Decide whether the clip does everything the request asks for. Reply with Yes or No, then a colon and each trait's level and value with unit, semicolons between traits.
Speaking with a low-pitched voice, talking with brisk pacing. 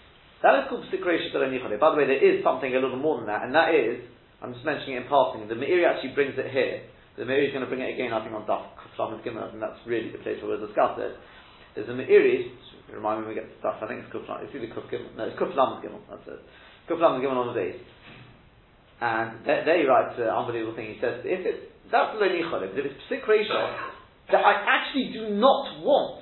No: very high, 260 Hz; fast, 230 wpm